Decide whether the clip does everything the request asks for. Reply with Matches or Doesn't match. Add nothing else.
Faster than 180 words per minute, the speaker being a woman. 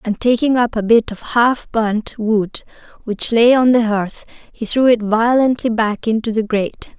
Matches